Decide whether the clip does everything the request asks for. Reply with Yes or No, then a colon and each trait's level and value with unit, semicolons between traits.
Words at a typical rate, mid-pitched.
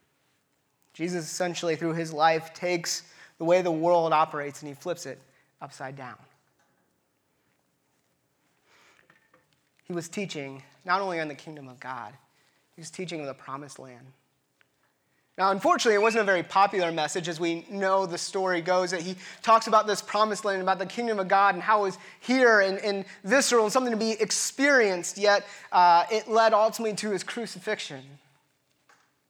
Yes: average, 165 wpm; medium, 180 Hz